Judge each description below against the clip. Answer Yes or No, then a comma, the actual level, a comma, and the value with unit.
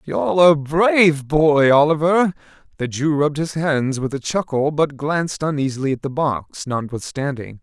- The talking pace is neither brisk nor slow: Yes, average, 155 wpm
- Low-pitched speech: No, medium, 150 Hz